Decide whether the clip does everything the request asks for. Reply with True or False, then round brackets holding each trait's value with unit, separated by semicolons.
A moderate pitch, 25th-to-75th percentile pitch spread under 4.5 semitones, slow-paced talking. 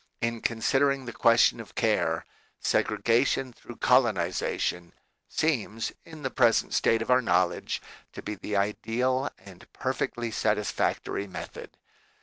False (115 Hz; 3.7 semitones; 125 wpm)